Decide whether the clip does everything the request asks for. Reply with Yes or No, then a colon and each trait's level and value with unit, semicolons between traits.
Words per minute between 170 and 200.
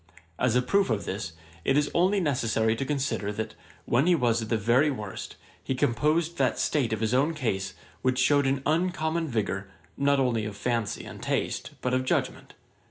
Yes: average, 190 wpm